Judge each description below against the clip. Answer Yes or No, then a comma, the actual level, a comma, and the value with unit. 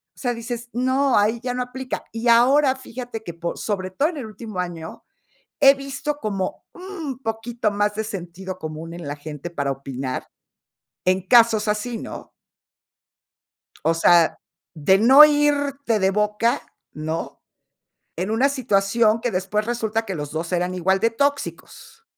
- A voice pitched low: No, high, 220 Hz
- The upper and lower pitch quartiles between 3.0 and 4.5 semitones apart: No, wide, 5.6 semitones